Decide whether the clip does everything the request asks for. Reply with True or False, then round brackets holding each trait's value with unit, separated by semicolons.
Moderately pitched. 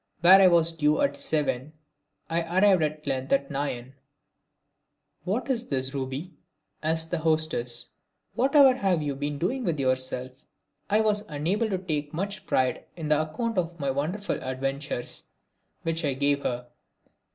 True (155 Hz)